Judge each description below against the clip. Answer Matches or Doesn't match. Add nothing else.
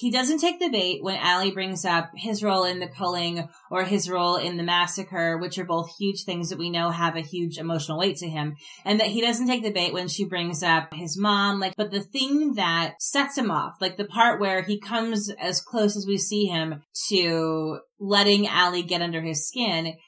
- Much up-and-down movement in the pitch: Doesn't match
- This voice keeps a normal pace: Doesn't match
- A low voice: Doesn't match